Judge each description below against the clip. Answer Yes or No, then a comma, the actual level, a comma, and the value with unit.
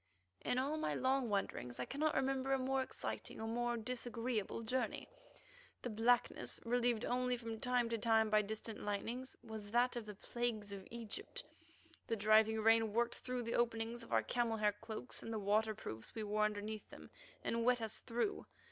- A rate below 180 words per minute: No, average, 185 wpm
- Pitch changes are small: Yes, narrow, 2.3 semitones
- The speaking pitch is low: No, high, 230 Hz